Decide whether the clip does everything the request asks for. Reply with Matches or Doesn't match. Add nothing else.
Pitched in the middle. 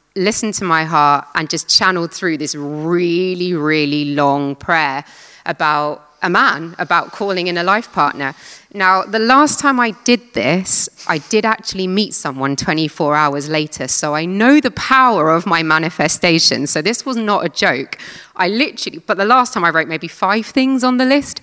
Matches